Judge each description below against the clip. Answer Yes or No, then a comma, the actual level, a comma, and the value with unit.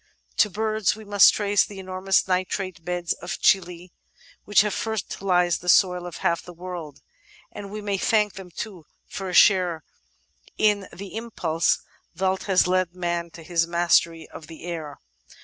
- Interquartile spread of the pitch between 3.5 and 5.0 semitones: No, average, 2.7 semitones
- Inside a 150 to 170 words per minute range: Yes, average, 165 wpm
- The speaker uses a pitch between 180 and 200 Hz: Yes, medium, 185 Hz